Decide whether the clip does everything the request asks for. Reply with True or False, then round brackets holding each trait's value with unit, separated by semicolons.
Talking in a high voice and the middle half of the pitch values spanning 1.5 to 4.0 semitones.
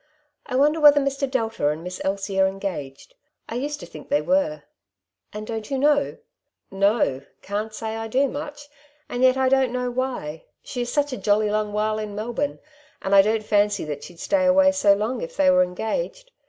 False (225 Hz; 5.5 semitones)